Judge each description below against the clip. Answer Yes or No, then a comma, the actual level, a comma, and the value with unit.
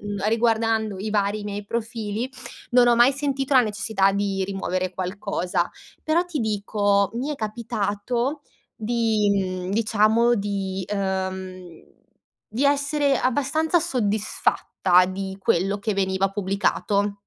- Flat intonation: No, average, 3.4 semitones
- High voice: Yes, high, 210 Hz